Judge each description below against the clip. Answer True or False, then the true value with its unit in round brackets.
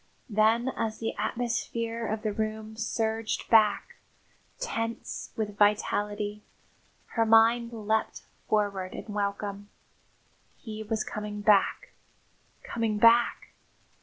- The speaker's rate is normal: False (105 wpm)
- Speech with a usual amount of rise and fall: False (1.6 semitones)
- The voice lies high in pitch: True (220 Hz)